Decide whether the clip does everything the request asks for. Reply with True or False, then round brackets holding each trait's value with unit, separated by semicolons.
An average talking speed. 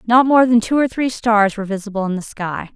False (260 wpm)